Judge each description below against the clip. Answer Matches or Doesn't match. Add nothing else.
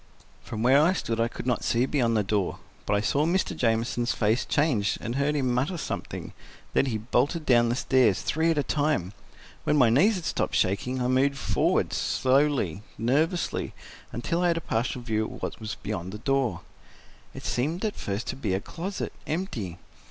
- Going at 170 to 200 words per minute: Matches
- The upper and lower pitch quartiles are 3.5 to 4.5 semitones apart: Doesn't match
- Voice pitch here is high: Doesn't match